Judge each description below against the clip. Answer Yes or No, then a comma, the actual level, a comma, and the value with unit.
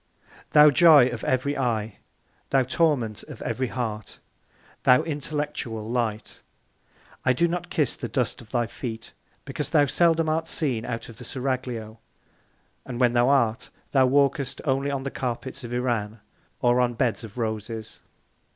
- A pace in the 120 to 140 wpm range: No, average, 155 wpm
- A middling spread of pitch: Yes, average, 3.4 semitones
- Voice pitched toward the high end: No, low, 125 Hz